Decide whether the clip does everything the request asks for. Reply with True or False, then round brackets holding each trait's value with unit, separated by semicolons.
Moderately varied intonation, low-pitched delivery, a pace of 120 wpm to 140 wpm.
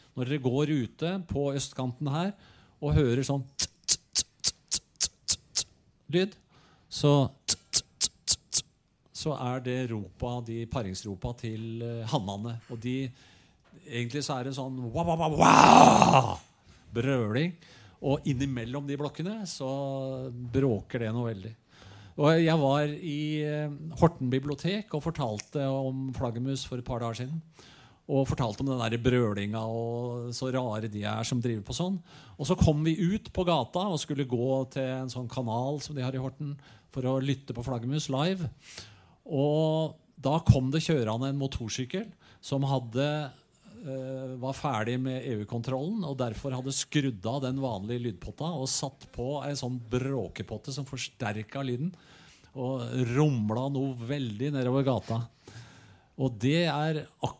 True (3.5 semitones; 130 Hz; 135 wpm)